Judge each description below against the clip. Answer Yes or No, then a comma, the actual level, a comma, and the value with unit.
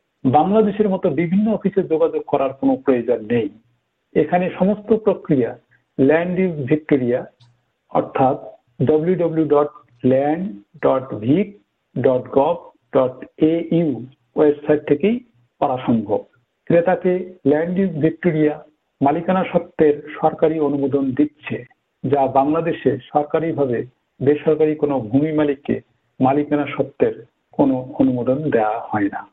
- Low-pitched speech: No, medium, 150 Hz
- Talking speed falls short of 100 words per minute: Yes, average, 80 wpm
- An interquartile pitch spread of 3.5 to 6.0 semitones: Yes, average, 4.0 semitones